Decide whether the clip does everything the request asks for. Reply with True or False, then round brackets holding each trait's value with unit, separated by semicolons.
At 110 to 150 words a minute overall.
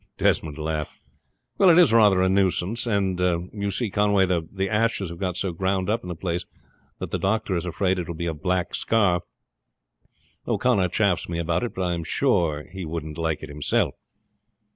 False (190 wpm)